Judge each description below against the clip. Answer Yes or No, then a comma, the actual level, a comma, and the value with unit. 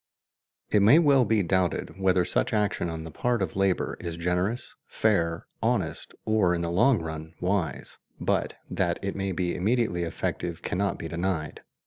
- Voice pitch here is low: Yes, very low, 90 Hz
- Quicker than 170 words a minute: No, average, 165 wpm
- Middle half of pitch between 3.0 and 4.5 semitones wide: Yes, average, 3.7 semitones